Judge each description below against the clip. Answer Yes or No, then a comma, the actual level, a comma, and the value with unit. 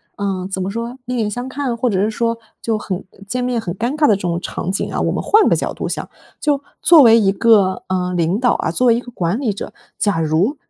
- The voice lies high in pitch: Yes, high, 220 Hz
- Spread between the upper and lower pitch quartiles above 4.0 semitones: Yes, average, 4.6 semitones